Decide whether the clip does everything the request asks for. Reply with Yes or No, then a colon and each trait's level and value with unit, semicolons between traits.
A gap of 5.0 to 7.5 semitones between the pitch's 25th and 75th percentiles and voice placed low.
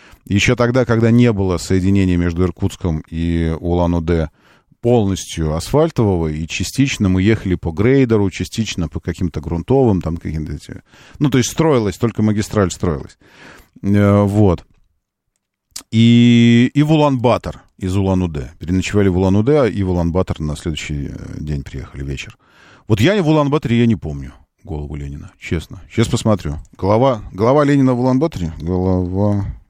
Yes: wide, 5.6 semitones; very low, 95 Hz